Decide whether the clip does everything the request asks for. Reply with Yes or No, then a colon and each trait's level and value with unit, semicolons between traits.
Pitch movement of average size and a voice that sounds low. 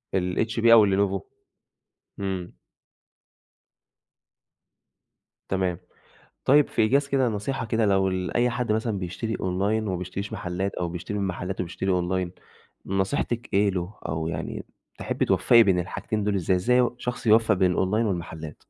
Yes: average, 3.6 semitones; very low, 95 Hz